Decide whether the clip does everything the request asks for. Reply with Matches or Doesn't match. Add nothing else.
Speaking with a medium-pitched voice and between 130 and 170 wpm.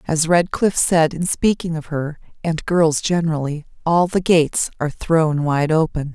Matches